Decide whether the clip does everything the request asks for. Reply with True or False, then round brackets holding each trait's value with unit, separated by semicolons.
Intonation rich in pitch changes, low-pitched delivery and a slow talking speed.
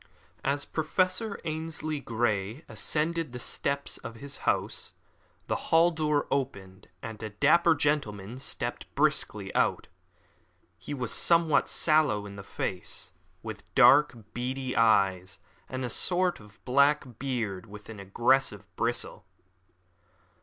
True (6.2 semitones; 130 Hz; 120 wpm)